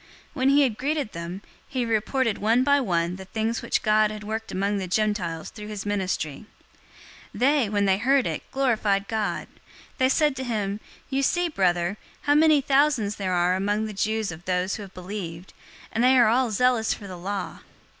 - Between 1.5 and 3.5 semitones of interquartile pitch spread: No, average, 4.9 semitones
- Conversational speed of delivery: Yes, average, 195 wpm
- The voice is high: Yes, high, 215 Hz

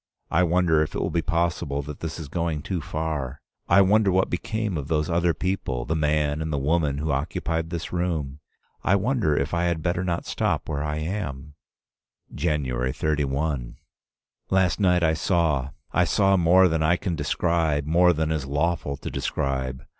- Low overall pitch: Yes, very low, 80 Hz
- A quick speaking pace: No, average, 180 wpm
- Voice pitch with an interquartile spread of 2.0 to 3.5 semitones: Yes, average, 3.1 semitones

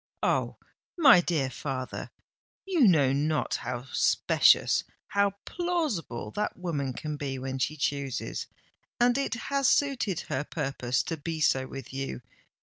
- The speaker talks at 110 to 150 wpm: Yes, slow, 135 wpm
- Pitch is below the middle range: No, medium, 150 Hz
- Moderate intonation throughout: No, wide, 7.9 semitones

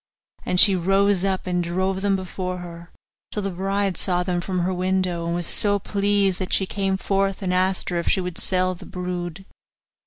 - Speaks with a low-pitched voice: No, medium, 185 Hz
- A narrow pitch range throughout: Yes, narrow, 1.5 semitones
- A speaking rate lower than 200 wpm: No, fast, 205 wpm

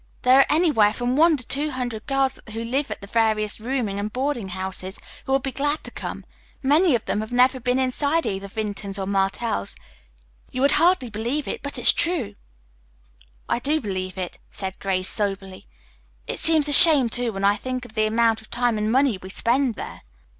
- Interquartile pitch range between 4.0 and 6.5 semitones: Yes, average, 4.9 semitones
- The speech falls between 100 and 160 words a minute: No, average, 200 wpm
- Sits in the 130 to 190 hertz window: No, high, 240 Hz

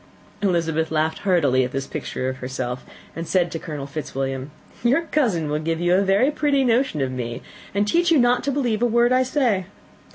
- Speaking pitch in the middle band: Yes, medium, 175 Hz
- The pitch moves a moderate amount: No, wide, 8.9 semitones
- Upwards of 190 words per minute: Yes, average, 200 wpm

